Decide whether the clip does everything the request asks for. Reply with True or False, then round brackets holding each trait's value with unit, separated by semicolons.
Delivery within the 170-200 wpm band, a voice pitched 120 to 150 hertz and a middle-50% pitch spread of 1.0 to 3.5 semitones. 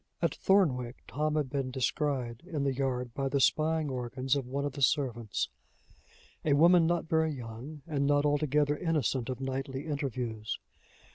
False (160 wpm; 140 Hz; 2.9 semitones)